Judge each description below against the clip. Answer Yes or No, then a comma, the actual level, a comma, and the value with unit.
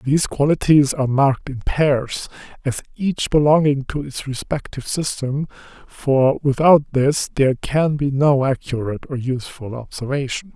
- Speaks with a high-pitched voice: No, medium, 140 Hz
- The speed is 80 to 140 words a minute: Yes, slow, 135 wpm